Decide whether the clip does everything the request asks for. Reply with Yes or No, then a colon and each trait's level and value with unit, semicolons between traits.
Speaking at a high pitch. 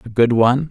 No: low, 120 Hz